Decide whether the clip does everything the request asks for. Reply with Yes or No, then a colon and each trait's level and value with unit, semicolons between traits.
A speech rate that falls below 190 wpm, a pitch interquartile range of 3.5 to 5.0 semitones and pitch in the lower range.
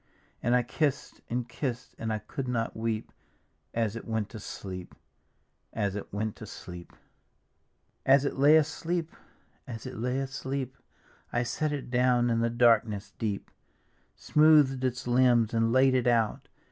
No: average, 160 wpm; average, 2.8 semitones; low, 120 Hz